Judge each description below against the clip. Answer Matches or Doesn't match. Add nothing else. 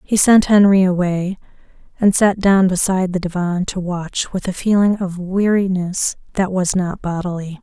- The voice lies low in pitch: Doesn't match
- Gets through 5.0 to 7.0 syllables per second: Doesn't match